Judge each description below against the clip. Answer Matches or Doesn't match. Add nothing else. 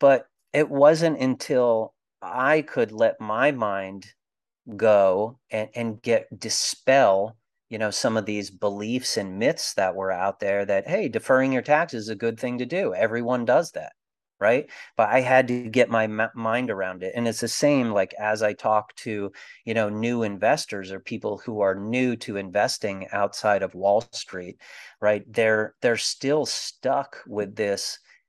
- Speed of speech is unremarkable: Matches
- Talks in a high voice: Doesn't match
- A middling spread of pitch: Matches